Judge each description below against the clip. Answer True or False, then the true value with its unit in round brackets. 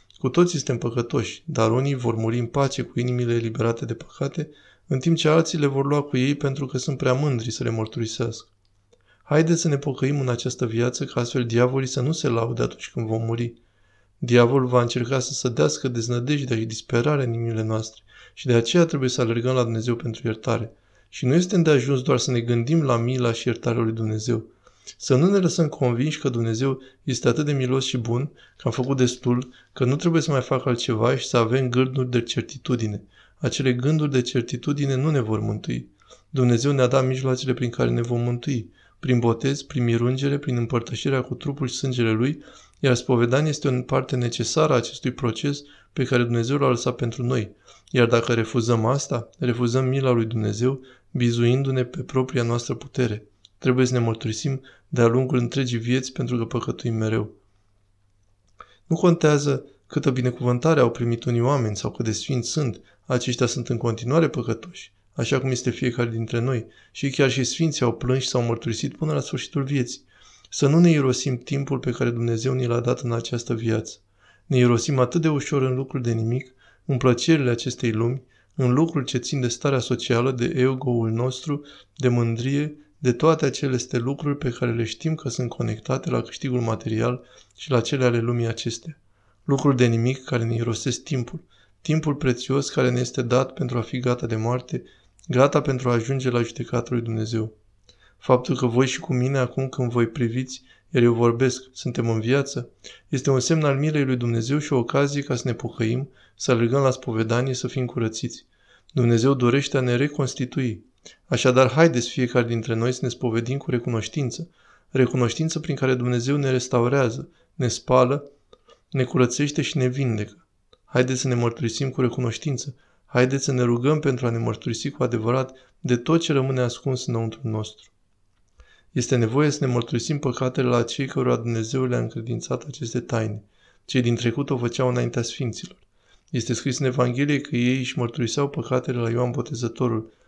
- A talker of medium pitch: False (125 Hz)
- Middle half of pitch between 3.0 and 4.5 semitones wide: False (2.6 semitones)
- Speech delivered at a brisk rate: True (185 wpm)